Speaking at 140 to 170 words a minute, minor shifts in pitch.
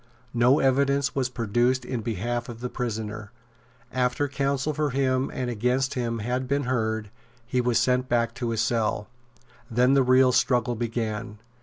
Yes: average, 160 wpm; narrow, 2.0 semitones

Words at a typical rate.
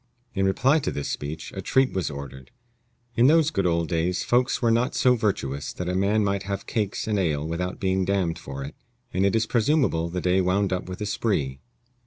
No: fast, 220 wpm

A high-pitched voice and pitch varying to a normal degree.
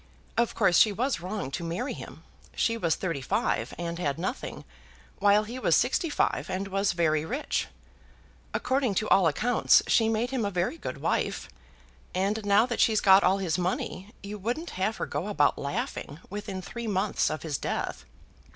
Yes: high, 195 Hz; average, 4.5 semitones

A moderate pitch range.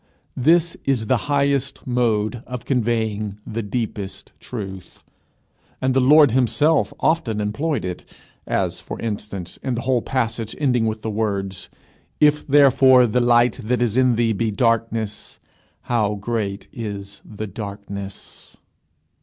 Yes: average, 3.6 semitones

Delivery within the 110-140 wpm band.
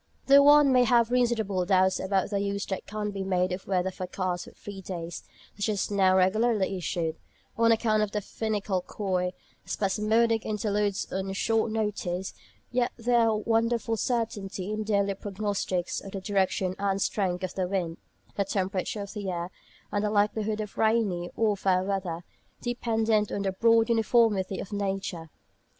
No: average, 170 wpm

